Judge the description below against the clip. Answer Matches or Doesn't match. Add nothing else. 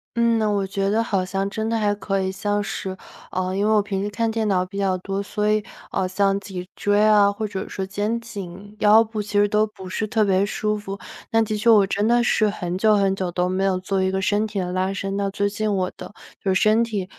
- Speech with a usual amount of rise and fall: Doesn't match